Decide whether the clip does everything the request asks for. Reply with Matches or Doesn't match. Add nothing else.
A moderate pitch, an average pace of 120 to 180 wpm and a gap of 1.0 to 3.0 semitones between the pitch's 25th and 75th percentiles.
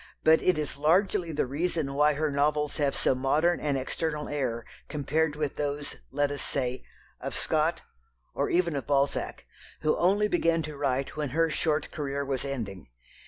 Matches